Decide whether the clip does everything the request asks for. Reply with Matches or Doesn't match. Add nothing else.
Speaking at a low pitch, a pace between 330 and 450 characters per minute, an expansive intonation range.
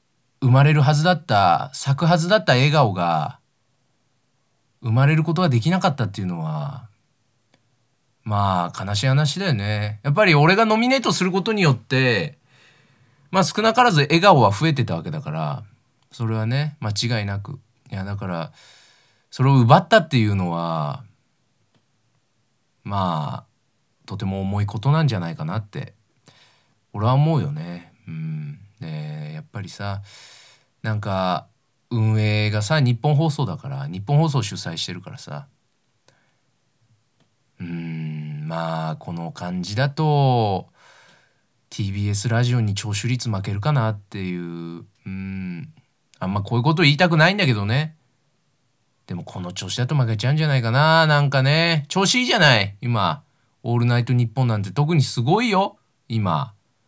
Doesn't match